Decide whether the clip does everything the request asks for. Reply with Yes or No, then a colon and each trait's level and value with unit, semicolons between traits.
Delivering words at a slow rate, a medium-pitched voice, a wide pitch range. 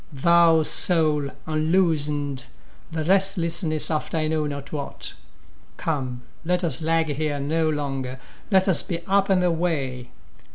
No: slow, 130 wpm; medium, 155 Hz; average, 2.9 semitones